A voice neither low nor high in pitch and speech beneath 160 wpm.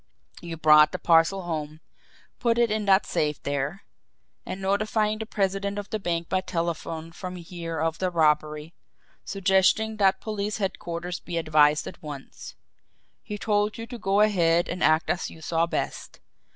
No: medium, 175 Hz; average, 165 wpm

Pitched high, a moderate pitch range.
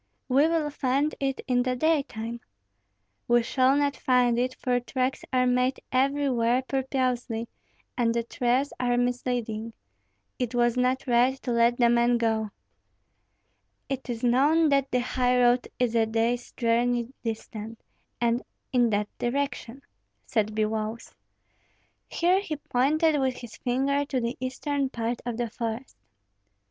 No: high, 245 Hz; narrow, 2.2 semitones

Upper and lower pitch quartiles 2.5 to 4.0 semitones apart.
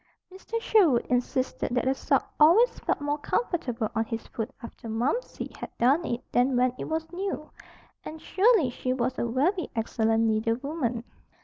No: wide, 5.5 semitones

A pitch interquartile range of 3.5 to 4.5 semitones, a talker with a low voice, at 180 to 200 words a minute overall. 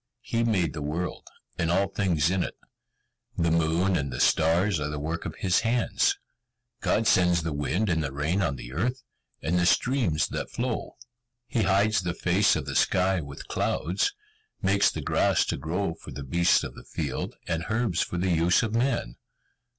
Yes: average, 3.9 semitones; very low, 90 Hz; average, 190 wpm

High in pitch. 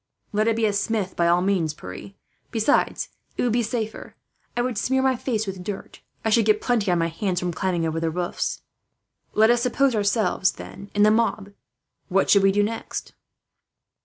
Yes: high, 205 Hz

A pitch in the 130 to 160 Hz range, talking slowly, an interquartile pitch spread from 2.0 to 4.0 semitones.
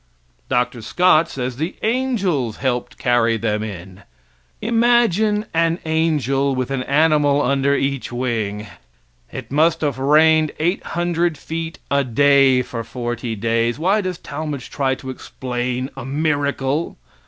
No: medium, 140 Hz; slow, 130 wpm; average, 4.7 semitones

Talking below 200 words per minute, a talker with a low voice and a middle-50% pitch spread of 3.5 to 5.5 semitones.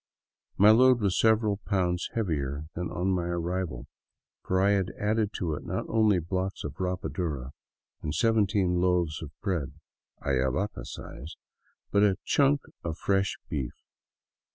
Yes: average, 160 wpm; very low, 90 Hz; average, 3.9 semitones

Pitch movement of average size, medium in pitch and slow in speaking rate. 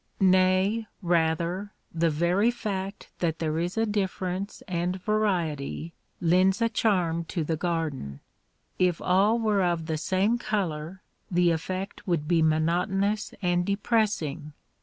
Yes: average, 3.3 semitones; medium, 180 Hz; slow, 125 wpm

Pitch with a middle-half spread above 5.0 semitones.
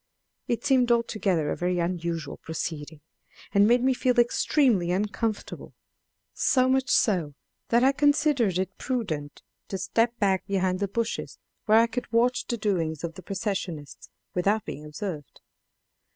Yes: wide, 5.6 semitones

